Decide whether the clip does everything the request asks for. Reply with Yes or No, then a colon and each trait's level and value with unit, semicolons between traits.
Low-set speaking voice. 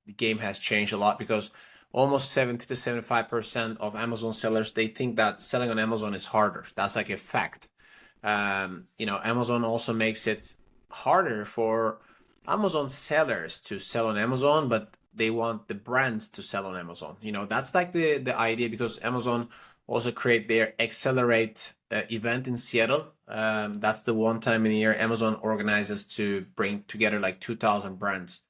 Yes: low, 115 Hz